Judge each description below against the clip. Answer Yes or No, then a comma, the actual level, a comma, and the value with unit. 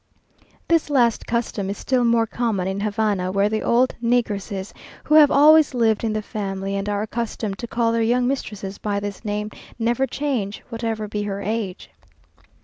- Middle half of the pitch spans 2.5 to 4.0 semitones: Yes, average, 2.9 semitones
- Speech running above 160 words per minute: Yes, average, 175 wpm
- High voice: Yes, high, 220 Hz